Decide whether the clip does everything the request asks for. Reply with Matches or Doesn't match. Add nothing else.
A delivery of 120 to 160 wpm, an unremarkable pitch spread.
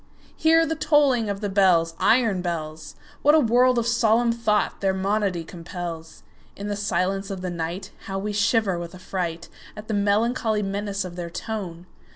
Matches